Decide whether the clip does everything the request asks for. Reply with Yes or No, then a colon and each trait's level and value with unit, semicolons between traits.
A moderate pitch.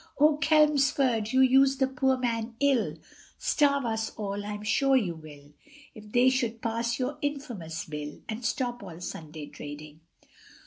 No: high, 235 Hz